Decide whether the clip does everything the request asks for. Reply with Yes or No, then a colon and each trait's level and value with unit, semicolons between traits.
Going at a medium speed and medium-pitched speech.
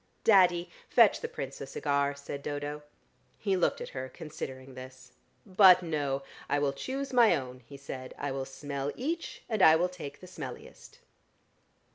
Yes: average, 165 wpm; medium, 145 Hz